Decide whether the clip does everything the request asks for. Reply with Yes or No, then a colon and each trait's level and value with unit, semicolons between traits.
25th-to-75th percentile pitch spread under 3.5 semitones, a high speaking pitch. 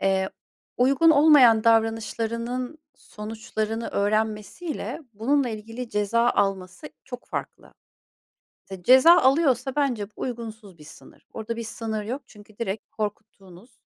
Yes: average, 3.1 semitones; high, 225 Hz